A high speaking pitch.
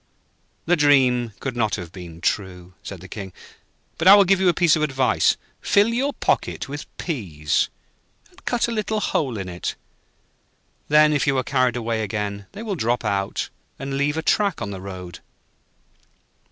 No: low, 130 Hz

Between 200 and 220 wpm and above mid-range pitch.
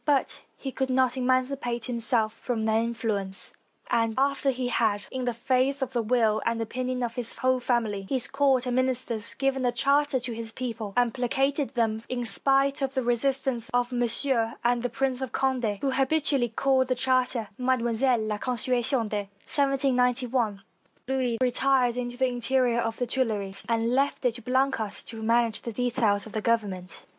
No: average, 175 wpm; high, 245 Hz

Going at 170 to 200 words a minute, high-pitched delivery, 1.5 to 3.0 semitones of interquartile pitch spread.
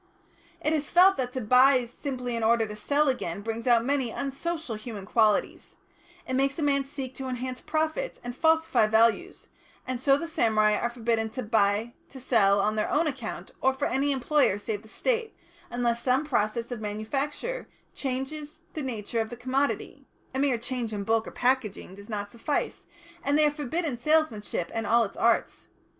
No: average, 185 wpm; very high, 250 Hz; average, 4.3 semitones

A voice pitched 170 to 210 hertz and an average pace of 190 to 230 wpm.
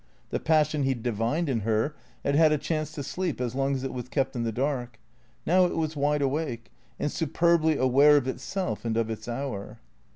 No: medium, 140 Hz; fast, 205 wpm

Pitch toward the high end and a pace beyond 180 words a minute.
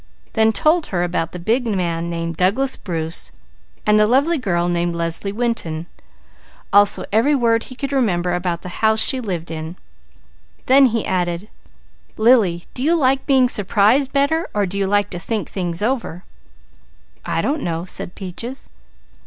No: high, 205 Hz; average, 165 wpm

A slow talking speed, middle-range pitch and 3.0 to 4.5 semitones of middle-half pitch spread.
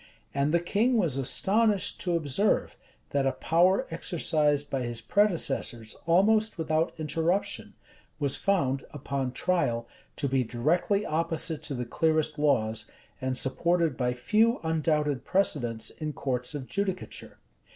No: slow, 130 wpm; medium, 155 Hz; average, 5.0 semitones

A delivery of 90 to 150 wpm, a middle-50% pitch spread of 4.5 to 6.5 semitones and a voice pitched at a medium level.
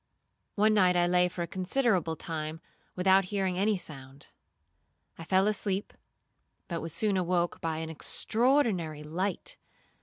No: average, 140 wpm; average, 3.5 semitones; medium, 180 Hz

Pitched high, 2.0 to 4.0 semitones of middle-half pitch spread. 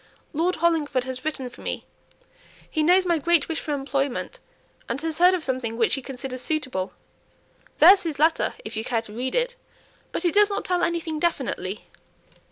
No: very high, 300 Hz; average, 5.0 semitones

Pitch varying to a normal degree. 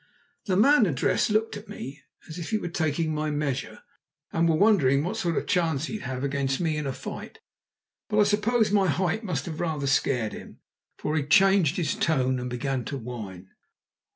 No: wide, 6.2 semitones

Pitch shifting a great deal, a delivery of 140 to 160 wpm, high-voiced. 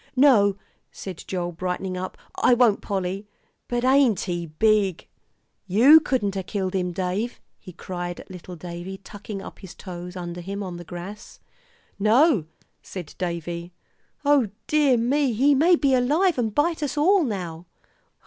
Yes: wide, 6.1 semitones; average, 155 wpm; high, 200 Hz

